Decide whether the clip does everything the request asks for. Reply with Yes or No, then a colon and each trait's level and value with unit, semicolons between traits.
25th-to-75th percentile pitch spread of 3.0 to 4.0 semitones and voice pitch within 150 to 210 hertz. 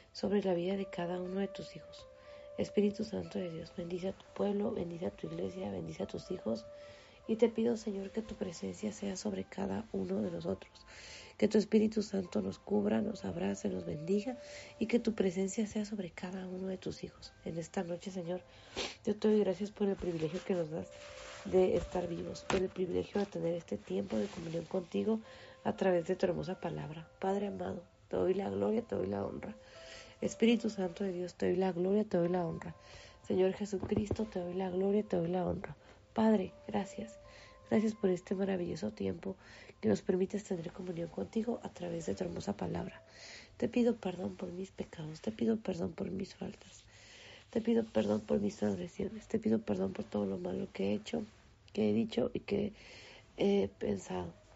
No: average, 4.4 semitones; medium, 185 Hz